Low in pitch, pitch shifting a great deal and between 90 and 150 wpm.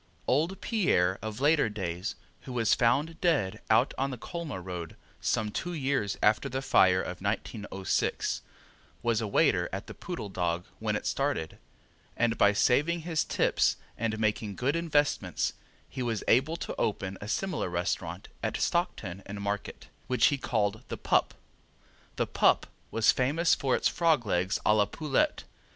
No: low, 115 Hz; wide, 6.2 semitones; average, 160 wpm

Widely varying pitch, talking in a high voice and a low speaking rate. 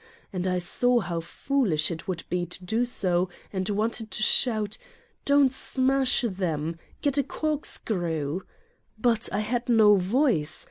No: wide, 5.7 semitones; high, 210 Hz; average, 150 wpm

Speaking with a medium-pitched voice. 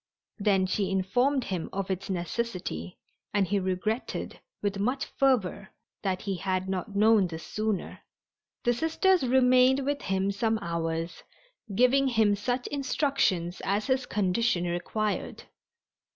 No: high, 205 Hz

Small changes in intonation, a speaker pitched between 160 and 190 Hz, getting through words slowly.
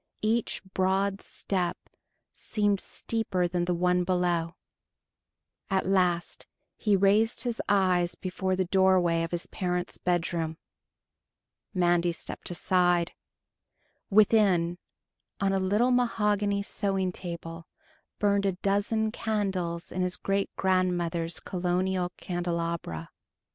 Yes: narrow, 2.3 semitones; medium, 185 Hz; slow, 105 wpm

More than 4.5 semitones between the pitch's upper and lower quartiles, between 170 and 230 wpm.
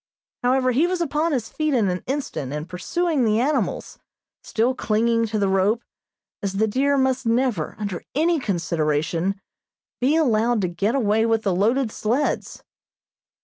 No: average, 5.2 semitones; average, 155 wpm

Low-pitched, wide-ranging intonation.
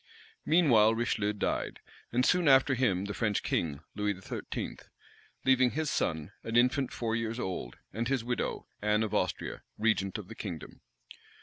No: low, 115 Hz; average, 3.7 semitones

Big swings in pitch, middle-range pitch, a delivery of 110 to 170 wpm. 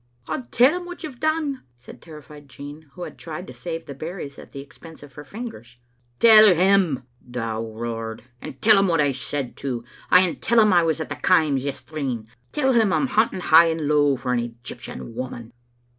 No: wide, 7.2 semitones; medium, 155 Hz; fast, 205 wpm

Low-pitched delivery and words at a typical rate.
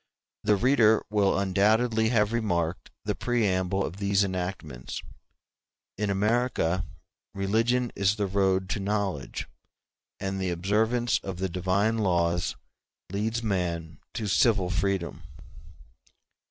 No: low, 100 Hz; slow, 115 wpm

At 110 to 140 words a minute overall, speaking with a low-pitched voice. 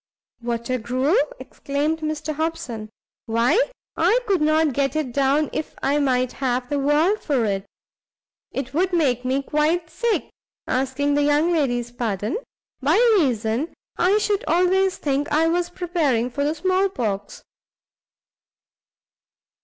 No: slow, 135 wpm; very high, 290 Hz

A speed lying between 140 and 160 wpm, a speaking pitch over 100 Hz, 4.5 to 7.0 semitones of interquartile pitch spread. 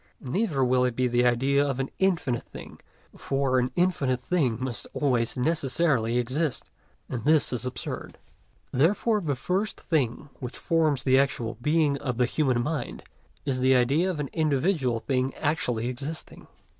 No: average, 155 wpm; low, 135 Hz; average, 3.8 semitones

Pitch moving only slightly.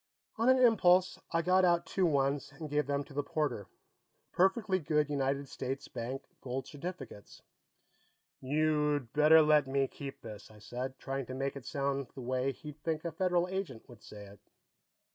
No: average, 3.6 semitones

